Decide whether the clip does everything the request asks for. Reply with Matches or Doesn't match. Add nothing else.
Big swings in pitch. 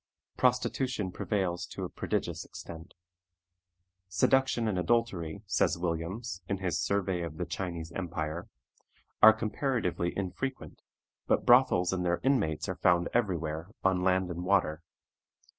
Doesn't match